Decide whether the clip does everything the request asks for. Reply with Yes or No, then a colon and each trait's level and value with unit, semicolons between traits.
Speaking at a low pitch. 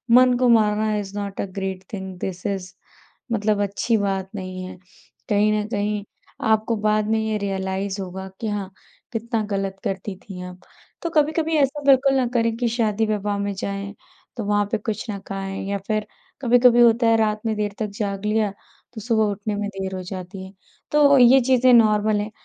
No: high, 210 Hz